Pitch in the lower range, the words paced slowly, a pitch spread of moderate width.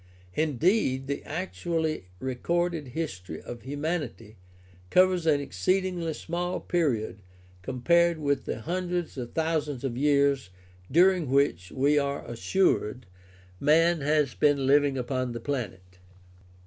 No: medium, 145 Hz; slow, 115 wpm; average, 4.8 semitones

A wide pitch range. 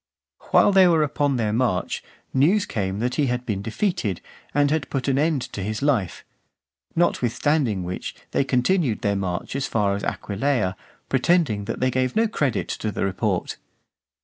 Yes: wide, 6.0 semitones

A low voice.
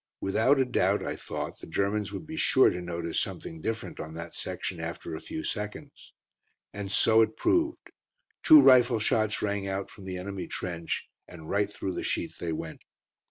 Yes: low, 100 Hz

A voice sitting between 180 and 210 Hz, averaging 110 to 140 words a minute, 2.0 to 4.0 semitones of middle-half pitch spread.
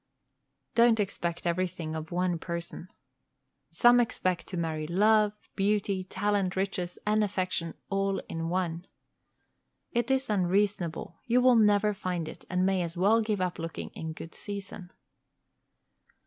Yes: medium, 185 Hz; slow, 135 wpm; average, 3.3 semitones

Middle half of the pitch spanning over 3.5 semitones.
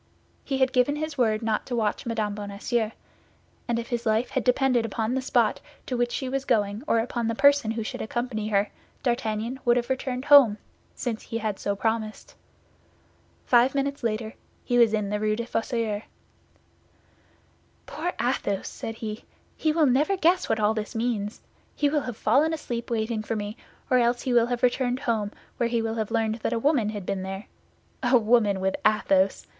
No: average, 2.8 semitones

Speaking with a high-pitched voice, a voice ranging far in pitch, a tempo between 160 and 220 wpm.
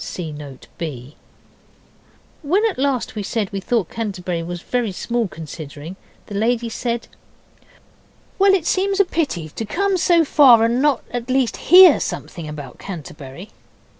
No: high, 225 Hz; wide, 8.9 semitones; average, 150 wpm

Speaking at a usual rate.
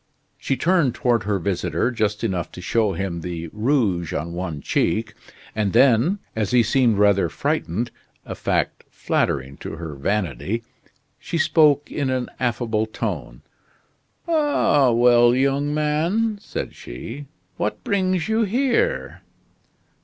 No: slow, 130 wpm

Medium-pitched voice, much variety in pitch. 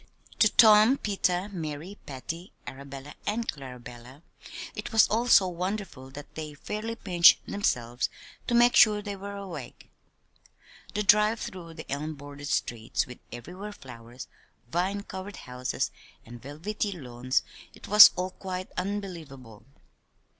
Yes: medium, 175 Hz; wide, 7.3 semitones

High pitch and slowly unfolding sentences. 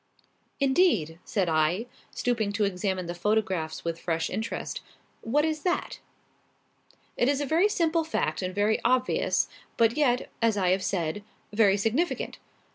No: high, 215 Hz; average, 145 wpm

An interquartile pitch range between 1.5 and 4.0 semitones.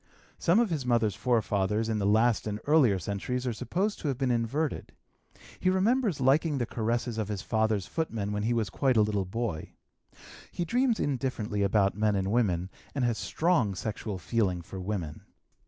No: average, 4.8 semitones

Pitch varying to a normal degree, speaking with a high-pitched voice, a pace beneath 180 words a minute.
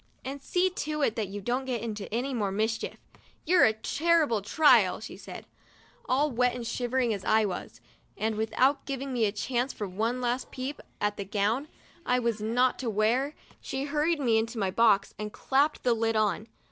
No: average, 3.8 semitones; high, 235 Hz; average, 195 wpm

